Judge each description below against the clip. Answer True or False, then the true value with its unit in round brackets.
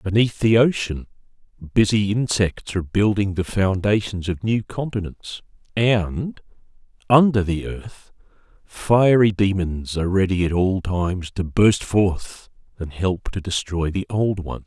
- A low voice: True (100 Hz)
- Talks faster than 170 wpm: False (135 wpm)